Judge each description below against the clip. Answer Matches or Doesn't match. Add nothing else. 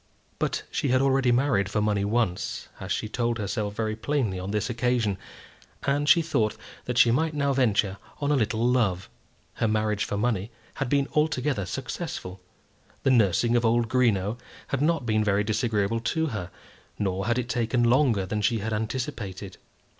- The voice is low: Matches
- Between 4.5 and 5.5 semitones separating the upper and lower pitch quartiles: Doesn't match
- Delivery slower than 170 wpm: Doesn't match